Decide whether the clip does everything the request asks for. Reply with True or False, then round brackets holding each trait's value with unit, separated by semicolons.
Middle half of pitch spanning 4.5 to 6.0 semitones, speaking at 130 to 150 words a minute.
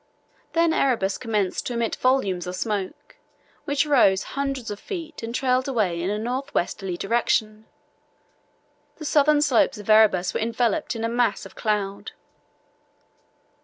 True (5.0 semitones; 145 wpm)